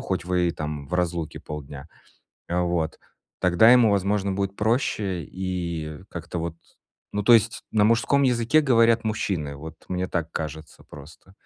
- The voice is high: No, very low, 90 Hz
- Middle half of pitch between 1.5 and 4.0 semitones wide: No, average, 4.8 semitones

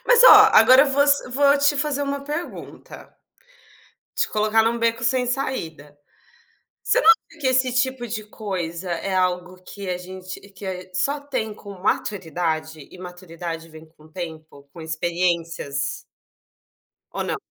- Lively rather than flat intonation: Yes, wide, 7.3 semitones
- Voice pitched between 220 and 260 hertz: No, high, 190 Hz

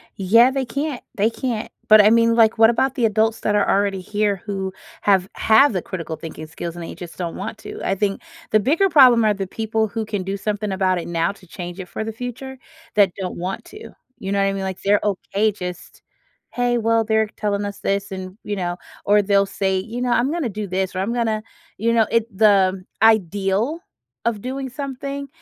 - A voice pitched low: No, high, 210 Hz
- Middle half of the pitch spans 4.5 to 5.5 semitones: No, average, 3.2 semitones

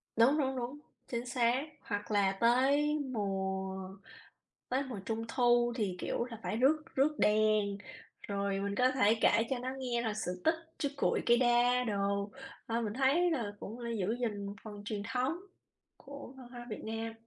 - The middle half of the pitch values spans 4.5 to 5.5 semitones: No, average, 3.8 semitones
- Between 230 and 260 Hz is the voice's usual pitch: Yes, high, 235 Hz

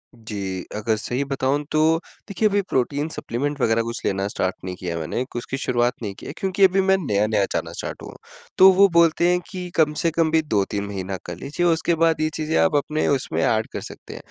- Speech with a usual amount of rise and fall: No, wide, 7.4 semitones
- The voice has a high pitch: No, medium, 140 Hz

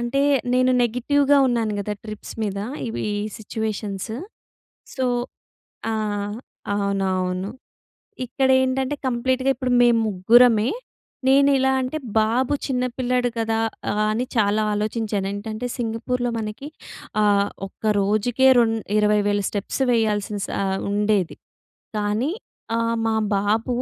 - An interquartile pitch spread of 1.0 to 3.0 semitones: No, average, 3.4 semitones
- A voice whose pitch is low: No, high, 225 Hz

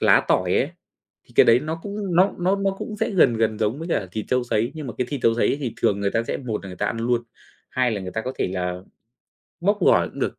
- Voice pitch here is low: Yes, low, 120 Hz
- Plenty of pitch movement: Yes, wide, 7.1 semitones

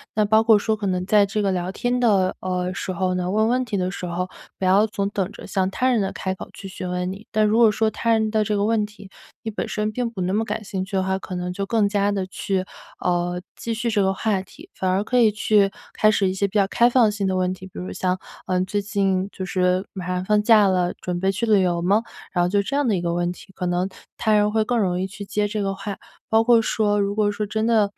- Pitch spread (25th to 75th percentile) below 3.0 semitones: Yes, narrow, 2.5 semitones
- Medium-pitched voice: No, high, 200 Hz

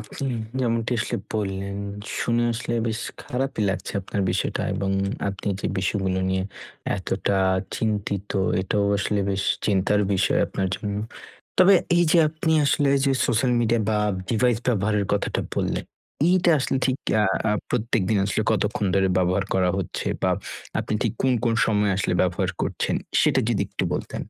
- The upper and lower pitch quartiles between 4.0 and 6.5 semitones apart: No, average, 3.4 semitones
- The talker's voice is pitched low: Yes, low, 105 Hz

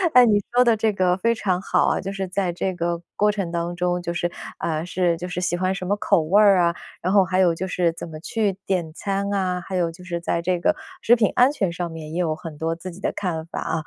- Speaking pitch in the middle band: Yes, medium, 180 Hz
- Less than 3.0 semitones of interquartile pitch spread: Yes, narrow, 2.4 semitones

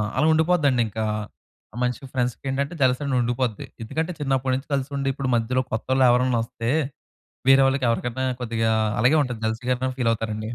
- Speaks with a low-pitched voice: Yes, low, 125 Hz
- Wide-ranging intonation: No, narrow, 2.5 semitones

